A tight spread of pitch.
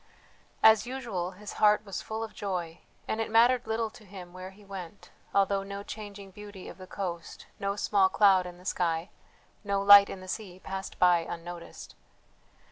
Yes: narrow, 2.3 semitones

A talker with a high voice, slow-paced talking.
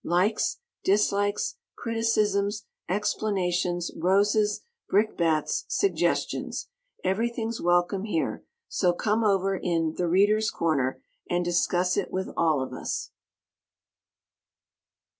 Yes: high, 195 Hz; slow, 95 wpm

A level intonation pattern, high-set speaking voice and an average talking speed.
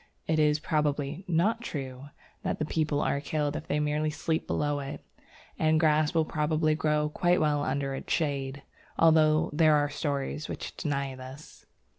No: narrow, 1.6 semitones; medium, 150 Hz; average, 160 wpm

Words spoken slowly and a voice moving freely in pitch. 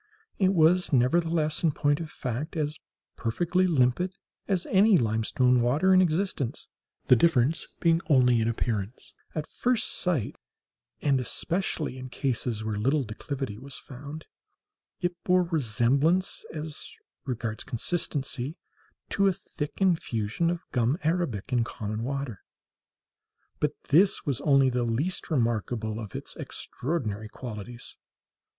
Yes: slow, 130 wpm; wide, 5.9 semitones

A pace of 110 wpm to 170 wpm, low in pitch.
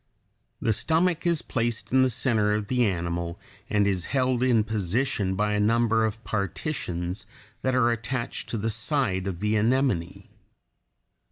Yes: average, 155 wpm; low, 110 Hz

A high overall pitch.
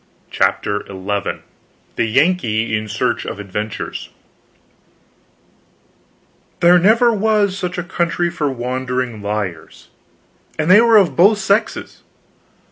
No: medium, 155 Hz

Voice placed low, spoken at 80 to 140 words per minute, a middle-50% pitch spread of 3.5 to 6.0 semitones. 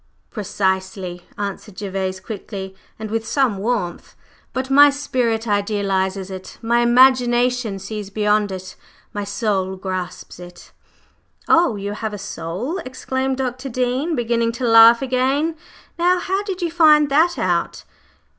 No: high, 225 Hz; slow, 135 wpm; average, 5.1 semitones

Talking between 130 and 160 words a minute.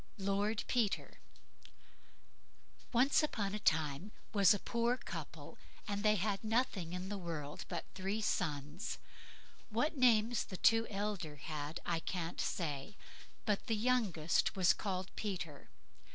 Yes: average, 140 wpm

